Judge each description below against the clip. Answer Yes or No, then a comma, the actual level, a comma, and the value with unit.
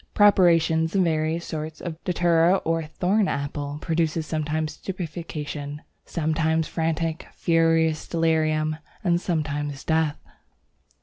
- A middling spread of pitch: No, narrow, 1.4 semitones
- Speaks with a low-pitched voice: No, medium, 160 Hz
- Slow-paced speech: Yes, slow, 105 wpm